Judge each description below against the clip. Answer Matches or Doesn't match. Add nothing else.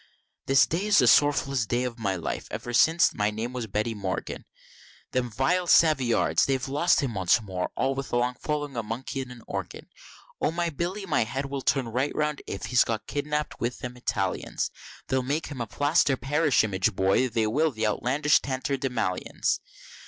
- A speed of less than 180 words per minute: Doesn't match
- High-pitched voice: Doesn't match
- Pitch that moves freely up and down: Doesn't match